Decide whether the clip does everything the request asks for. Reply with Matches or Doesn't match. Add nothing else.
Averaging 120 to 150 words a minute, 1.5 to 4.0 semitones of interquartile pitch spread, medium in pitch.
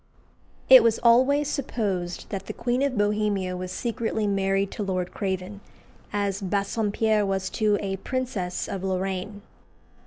Doesn't match